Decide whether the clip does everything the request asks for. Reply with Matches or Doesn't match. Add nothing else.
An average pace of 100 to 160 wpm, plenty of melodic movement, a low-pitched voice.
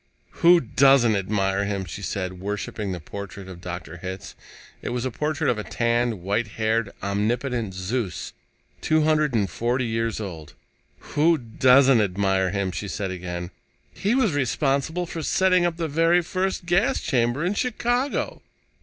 Matches